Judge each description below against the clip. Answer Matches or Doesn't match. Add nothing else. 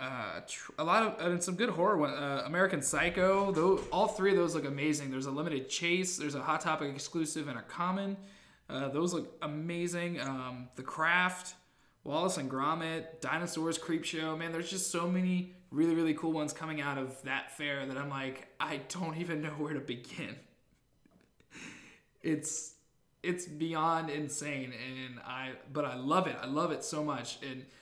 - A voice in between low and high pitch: Matches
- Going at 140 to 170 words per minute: Doesn't match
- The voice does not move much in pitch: Doesn't match